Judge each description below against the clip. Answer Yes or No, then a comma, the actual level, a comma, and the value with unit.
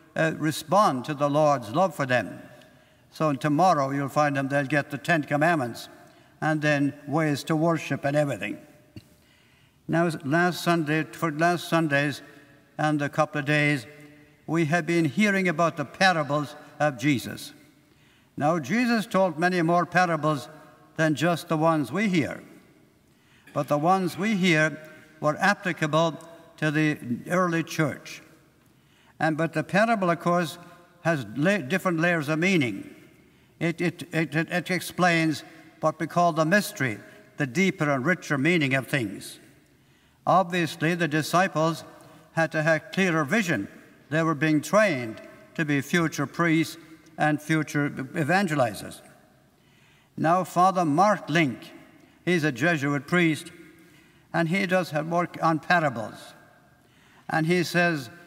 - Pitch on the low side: No, medium, 160 Hz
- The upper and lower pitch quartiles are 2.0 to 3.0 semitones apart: Yes, narrow, 2.6 semitones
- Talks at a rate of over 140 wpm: No, slow, 135 wpm